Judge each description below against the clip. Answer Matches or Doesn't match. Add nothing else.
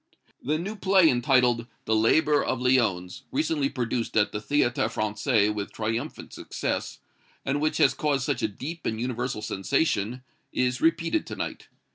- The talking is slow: Doesn't match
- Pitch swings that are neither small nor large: Matches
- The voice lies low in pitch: Matches